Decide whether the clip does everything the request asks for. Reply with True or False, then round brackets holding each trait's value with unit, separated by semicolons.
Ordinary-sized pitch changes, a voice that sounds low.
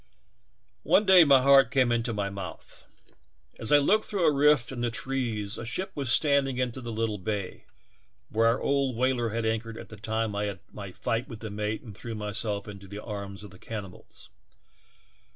True (4.0 semitones; 115 Hz)